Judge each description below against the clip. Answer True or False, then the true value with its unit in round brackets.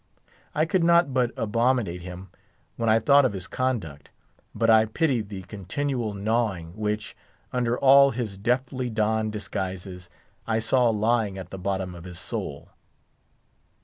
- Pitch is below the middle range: True (110 Hz)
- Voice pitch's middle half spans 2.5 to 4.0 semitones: False (4.5 semitones)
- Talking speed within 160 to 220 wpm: False (145 wpm)